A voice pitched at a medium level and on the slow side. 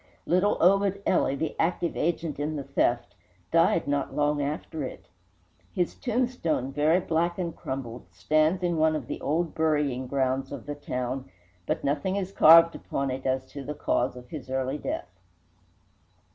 No: medium, 150 Hz; average, 165 wpm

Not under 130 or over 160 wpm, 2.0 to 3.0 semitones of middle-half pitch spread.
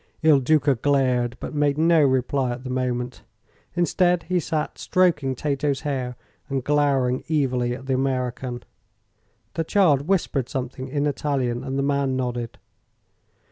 Yes: average, 140 wpm; average, 2.7 semitones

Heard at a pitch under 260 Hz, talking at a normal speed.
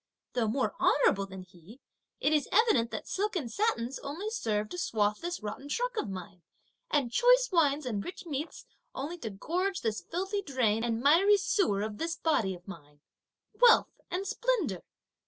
No: very high, 280 Hz; average, 175 wpm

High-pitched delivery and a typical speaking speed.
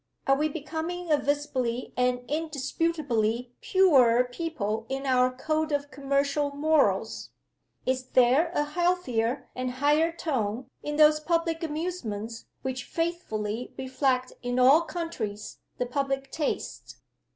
No: very high, 275 Hz; slow, 120 wpm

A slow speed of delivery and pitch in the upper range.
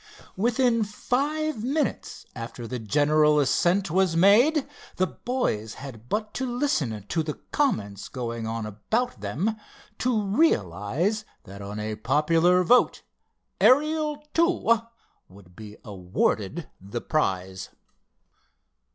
No: slow, 115 wpm; medium, 160 Hz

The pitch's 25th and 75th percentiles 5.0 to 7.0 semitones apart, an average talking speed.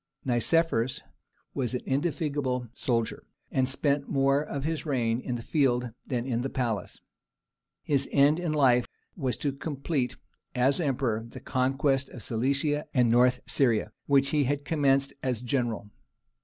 No: narrow, 2.4 semitones; average, 145 wpm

